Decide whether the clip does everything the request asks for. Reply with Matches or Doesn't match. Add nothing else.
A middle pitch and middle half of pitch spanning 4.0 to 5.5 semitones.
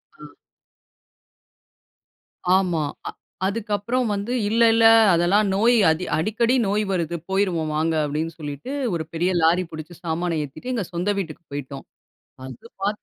Matches